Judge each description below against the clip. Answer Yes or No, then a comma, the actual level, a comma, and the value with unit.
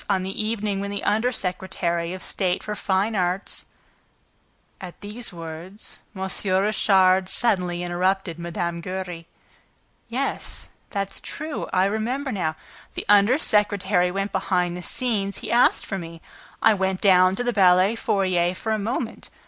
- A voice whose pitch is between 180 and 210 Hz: Yes, high, 190 Hz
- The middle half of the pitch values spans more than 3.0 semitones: No, average, 2.7 semitones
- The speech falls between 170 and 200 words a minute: No, average, 150 wpm